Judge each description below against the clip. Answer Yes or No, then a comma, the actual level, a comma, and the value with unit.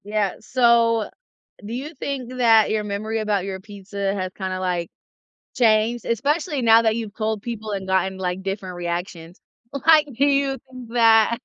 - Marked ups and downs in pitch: No, average, 3.7 semitones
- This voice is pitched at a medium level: No, high, 220 Hz